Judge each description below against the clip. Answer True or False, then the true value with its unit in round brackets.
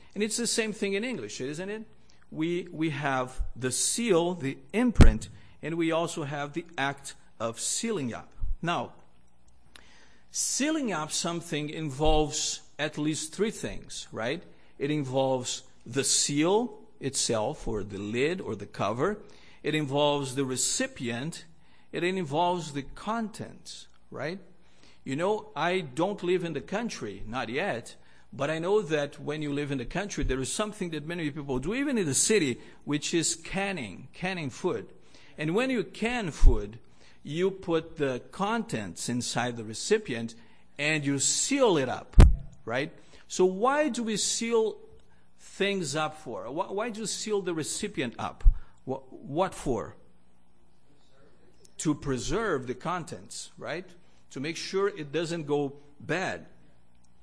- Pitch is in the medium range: True (155 Hz)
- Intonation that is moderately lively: False (6.7 semitones)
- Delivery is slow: False (145 wpm)